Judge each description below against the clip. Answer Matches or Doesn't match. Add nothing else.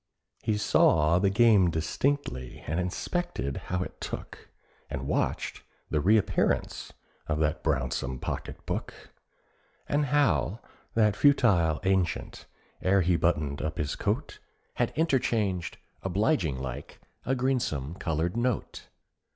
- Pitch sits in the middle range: Doesn't match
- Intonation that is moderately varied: Doesn't match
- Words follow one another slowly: Matches